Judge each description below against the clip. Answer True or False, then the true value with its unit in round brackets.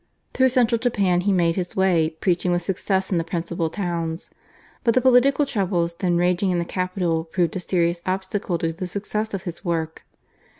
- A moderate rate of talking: True (185 wpm)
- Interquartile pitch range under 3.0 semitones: True (2.6 semitones)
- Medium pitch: True (180 Hz)